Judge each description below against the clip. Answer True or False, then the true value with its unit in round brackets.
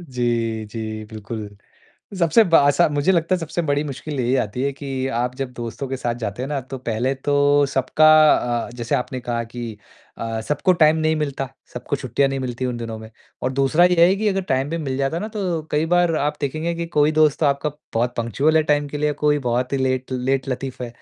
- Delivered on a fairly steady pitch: False (3.9 semitones)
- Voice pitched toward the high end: False (135 Hz)